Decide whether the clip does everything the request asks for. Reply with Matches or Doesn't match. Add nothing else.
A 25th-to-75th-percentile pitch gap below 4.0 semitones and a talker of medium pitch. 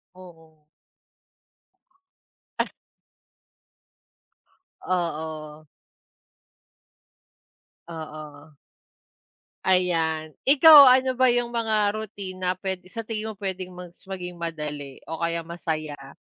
Doesn't match